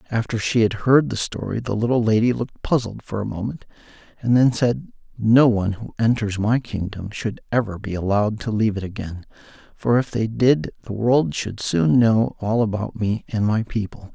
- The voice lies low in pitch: Yes, low, 110 Hz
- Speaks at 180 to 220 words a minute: Yes, average, 195 wpm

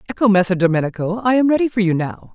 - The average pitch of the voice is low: No, high, 205 Hz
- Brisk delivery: Yes, fast, 230 wpm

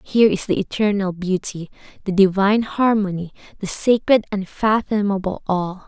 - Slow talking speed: Yes, slow, 125 wpm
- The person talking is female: Yes, female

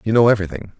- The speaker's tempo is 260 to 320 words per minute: No, fast, 225 wpm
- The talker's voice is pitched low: Yes, low, 105 Hz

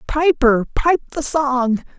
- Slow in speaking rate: Yes, slow, 120 wpm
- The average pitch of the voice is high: Yes, very high, 275 Hz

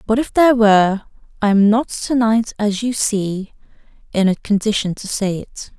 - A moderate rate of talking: Yes, average, 185 wpm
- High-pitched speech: Yes, high, 215 Hz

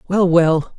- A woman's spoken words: No, male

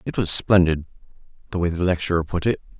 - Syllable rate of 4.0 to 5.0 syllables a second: No, 6.5 syllables/s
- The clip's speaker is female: No, male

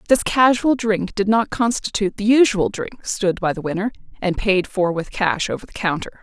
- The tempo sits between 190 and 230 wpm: Yes, average, 200 wpm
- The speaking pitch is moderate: No, high, 205 Hz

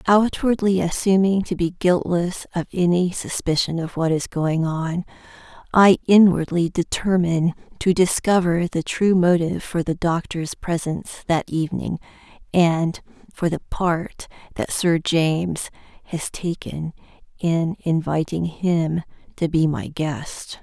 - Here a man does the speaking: No, female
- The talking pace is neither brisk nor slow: No, slow, 125 wpm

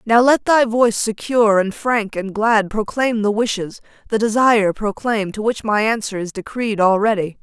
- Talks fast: No, average, 180 wpm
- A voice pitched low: No, high, 215 Hz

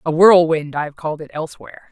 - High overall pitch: No, medium, 160 Hz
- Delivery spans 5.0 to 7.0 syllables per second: Yes, 6.7 syllables/s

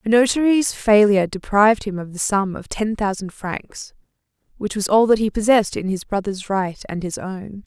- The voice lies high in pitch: Yes, high, 205 Hz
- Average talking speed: Yes, average, 195 wpm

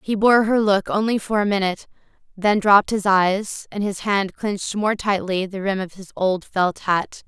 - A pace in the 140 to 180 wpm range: No, fast, 205 wpm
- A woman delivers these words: Yes, female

